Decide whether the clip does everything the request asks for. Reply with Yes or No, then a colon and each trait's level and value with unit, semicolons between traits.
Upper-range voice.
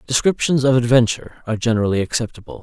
No: low, 120 Hz